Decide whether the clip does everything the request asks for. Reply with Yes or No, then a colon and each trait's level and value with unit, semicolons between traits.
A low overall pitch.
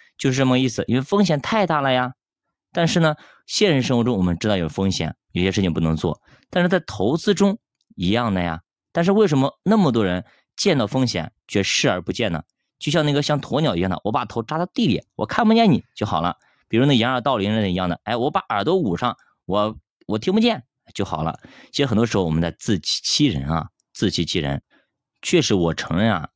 Yes: low, 120 Hz